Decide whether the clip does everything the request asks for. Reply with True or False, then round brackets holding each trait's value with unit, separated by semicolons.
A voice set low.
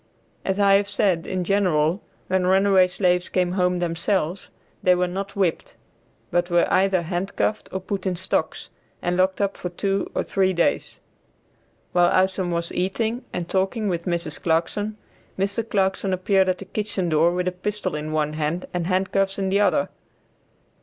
False (185 Hz)